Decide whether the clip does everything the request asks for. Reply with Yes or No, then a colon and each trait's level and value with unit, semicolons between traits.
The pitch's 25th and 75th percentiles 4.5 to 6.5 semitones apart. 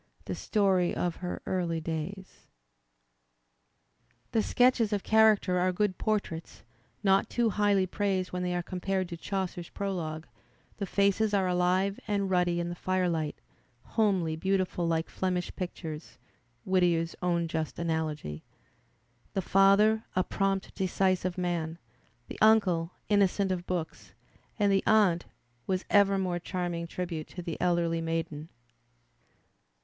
No: narrow, 2.5 semitones